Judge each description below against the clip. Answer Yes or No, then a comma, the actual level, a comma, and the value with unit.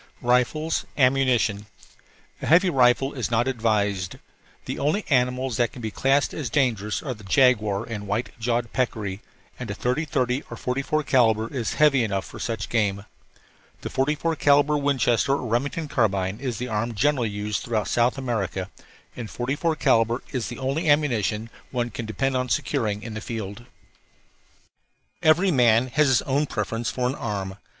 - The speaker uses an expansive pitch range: No, average, 3.9 semitones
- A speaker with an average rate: Yes, average, 165 wpm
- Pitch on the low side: Yes, low, 120 Hz